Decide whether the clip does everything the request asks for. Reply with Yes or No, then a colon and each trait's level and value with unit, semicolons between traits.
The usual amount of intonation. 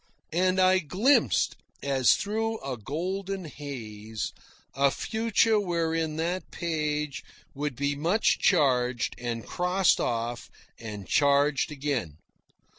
No: wide, 6.2 semitones